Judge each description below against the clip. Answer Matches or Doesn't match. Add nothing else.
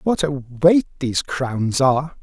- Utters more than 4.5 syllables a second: Doesn't match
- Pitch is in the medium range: Matches